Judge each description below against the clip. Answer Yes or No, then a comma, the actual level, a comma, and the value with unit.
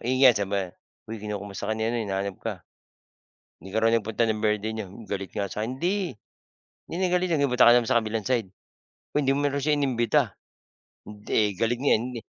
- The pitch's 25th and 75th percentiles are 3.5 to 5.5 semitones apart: Yes, average, 3.8 semitones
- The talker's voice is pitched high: No, low, 115 Hz